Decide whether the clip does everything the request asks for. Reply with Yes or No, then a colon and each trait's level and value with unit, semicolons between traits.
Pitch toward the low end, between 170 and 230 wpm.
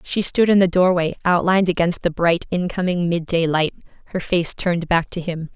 No: medium, 175 Hz; average, 195 wpm